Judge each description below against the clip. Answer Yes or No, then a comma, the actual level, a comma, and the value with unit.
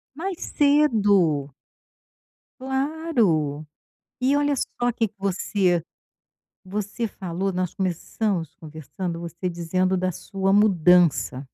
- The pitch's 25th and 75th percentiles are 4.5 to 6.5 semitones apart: Yes, average, 4.9 semitones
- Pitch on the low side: No, high, 190 Hz